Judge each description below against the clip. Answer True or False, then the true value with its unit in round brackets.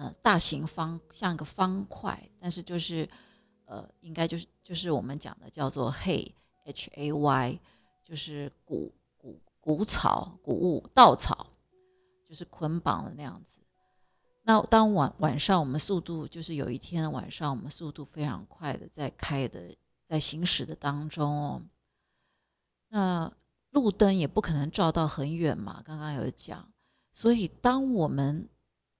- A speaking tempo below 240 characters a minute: True (215 characters per minute)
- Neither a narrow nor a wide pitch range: True (4.0 semitones)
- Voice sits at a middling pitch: True (160 Hz)